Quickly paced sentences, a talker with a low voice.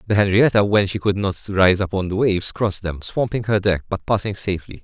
Yes: fast, 225 wpm; low, 100 Hz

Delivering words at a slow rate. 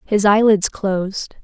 Yes: slow, 125 wpm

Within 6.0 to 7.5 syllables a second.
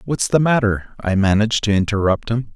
No: 5.5 syllables/s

